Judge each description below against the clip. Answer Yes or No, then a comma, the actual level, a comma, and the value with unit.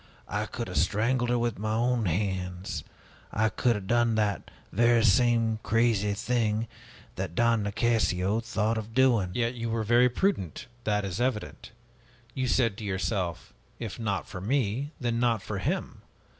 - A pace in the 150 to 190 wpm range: Yes, average, 160 wpm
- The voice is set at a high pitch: No, low, 110 Hz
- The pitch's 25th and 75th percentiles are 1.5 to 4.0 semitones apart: Yes, average, 2.9 semitones